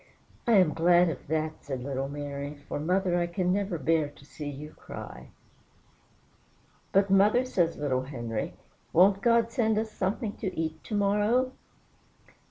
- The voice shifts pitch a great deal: Yes, wide, 5.7 semitones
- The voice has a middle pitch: Yes, medium, 175 Hz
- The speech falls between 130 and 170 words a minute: Yes, average, 160 wpm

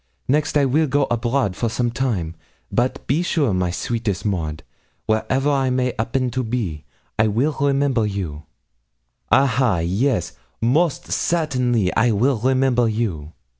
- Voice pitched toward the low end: Yes, low, 120 Hz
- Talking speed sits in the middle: Yes, average, 145 wpm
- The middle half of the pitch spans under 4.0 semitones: No, average, 4.6 semitones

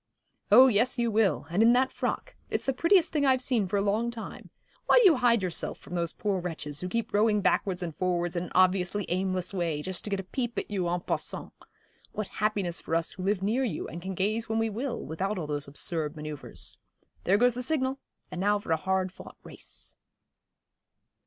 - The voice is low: No, high, 195 Hz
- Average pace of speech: No, fast, 215 wpm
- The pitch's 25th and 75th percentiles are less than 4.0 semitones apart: No, average, 4.7 semitones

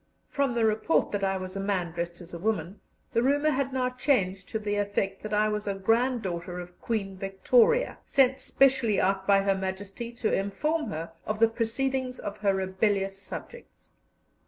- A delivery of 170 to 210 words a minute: Yes, average, 180 wpm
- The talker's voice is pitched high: Yes, high, 205 Hz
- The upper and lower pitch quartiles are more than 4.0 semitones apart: Yes, average, 4.6 semitones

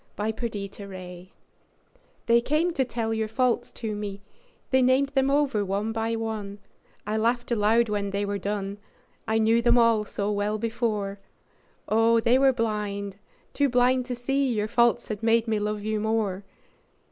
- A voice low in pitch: No, high, 220 Hz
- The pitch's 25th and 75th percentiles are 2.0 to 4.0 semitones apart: Yes, narrow, 2.6 semitones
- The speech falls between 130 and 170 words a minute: Yes, average, 160 wpm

